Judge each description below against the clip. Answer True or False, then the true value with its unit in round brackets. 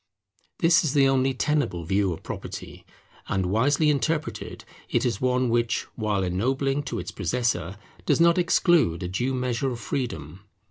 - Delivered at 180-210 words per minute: False (155 wpm)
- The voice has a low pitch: True (125 Hz)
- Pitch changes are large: True (6.2 semitones)